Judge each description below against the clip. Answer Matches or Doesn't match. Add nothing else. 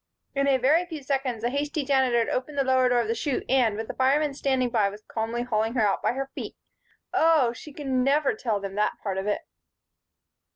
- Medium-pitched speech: Doesn't match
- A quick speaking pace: Matches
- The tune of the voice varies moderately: Matches